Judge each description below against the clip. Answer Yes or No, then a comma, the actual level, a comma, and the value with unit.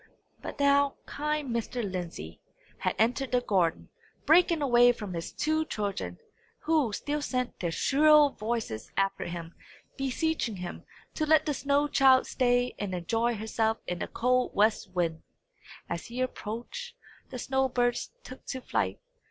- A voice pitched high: Yes, high, 245 Hz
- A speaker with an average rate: Yes, average, 150 wpm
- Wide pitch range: Yes, wide, 5.7 semitones